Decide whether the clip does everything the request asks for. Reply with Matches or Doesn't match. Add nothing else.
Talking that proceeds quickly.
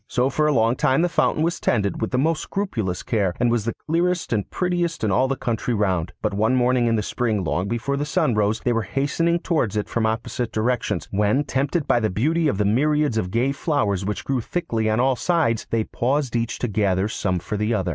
Matches